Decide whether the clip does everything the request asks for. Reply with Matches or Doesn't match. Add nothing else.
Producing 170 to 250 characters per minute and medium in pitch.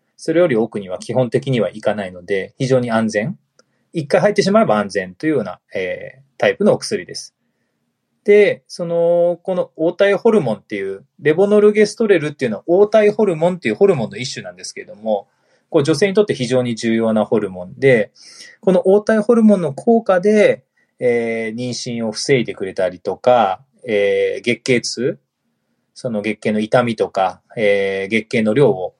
Doesn't match